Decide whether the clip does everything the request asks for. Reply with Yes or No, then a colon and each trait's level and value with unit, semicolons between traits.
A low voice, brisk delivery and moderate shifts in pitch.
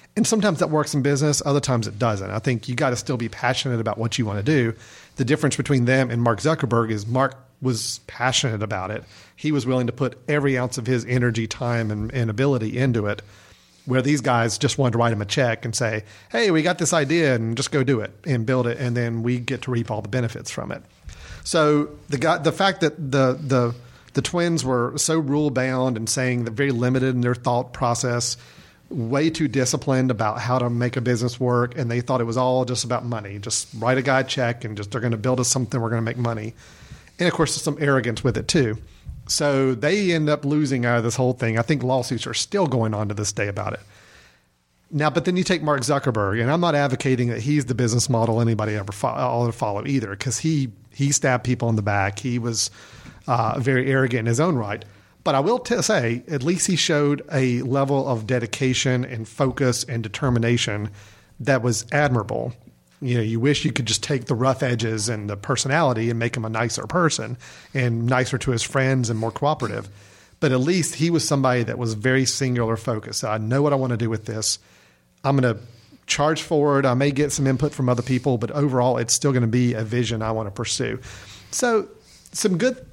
Yes: low, 125 Hz; fast, 230 wpm; average, 3.3 semitones